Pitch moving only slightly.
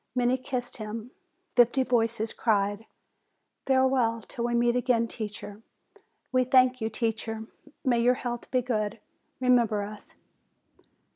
Yes: narrow, 2.2 semitones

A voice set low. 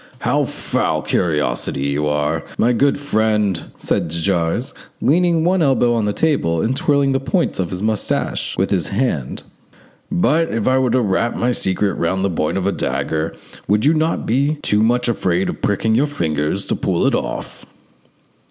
Yes: low, 105 Hz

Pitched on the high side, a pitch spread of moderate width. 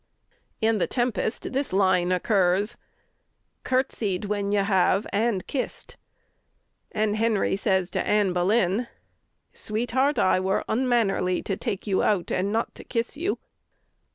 Yes: high, 205 Hz; average, 3.5 semitones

